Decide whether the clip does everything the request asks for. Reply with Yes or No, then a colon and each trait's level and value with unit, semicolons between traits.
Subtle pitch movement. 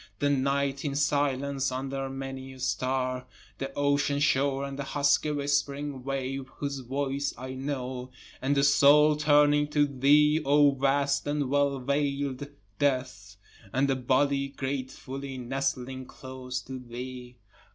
Yes: narrow, 1.5 semitones